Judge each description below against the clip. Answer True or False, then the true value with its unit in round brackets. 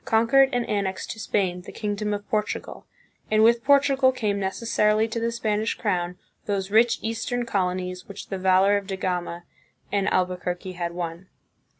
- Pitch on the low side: False (205 Hz)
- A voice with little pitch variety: False (3.5 semitones)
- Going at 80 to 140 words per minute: False (165 wpm)